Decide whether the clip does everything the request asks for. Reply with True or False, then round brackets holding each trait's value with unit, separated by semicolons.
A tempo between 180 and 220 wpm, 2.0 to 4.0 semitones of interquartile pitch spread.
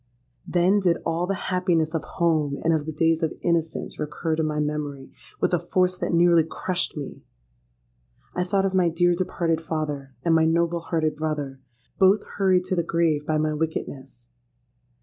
False (170 wpm; 2.5 semitones)